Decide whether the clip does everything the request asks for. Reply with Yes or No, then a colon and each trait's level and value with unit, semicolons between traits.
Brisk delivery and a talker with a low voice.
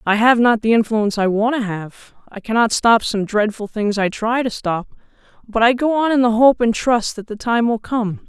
No: fast, 240 wpm; high, 225 Hz